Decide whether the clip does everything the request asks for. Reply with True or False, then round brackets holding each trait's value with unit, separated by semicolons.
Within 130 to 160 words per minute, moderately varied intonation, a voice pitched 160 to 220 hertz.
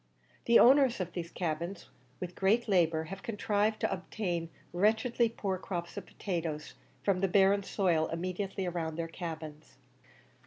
True (145 wpm; 3.3 semitones; 185 Hz)